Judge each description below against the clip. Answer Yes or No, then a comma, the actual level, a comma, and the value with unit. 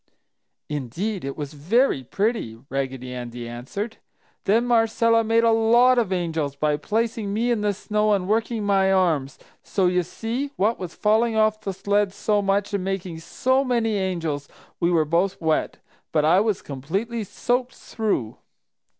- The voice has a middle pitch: No, high, 200 Hz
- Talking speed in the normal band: Yes, average, 160 wpm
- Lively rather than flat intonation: Yes, wide, 5.8 semitones